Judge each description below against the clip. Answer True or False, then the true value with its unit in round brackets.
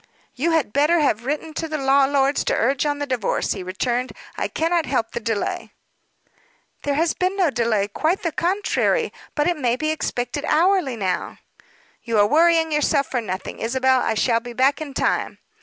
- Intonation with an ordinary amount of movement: True (5.0 semitones)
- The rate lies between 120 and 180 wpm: False (190 wpm)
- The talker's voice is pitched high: True (280 Hz)